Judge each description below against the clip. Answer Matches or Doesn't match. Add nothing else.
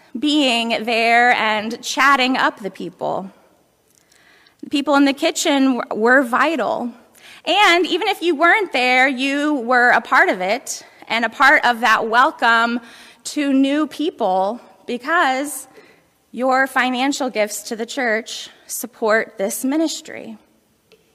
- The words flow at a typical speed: Doesn't match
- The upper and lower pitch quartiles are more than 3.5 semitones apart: Matches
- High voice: Matches